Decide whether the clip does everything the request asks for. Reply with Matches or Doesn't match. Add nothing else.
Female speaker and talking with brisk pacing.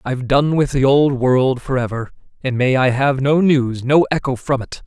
Doesn't match